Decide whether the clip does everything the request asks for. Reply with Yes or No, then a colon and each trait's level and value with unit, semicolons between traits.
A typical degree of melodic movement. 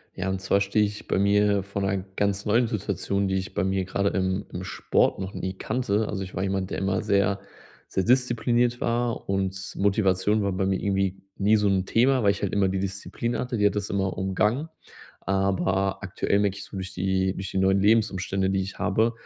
No: narrow, 1.5 semitones